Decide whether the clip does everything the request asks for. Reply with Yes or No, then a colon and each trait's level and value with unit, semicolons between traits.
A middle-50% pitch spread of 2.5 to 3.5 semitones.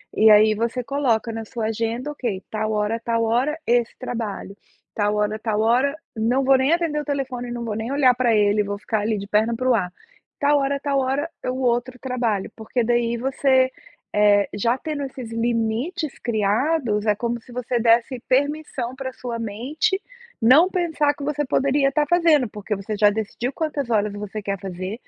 No: average, 3.9 semitones